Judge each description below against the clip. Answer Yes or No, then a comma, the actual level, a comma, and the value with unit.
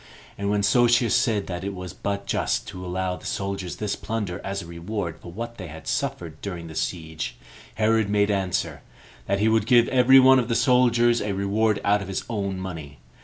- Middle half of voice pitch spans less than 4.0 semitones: Yes, average, 3.6 semitones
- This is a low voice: Yes, low, 100 Hz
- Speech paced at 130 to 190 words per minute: No, average, 200 wpm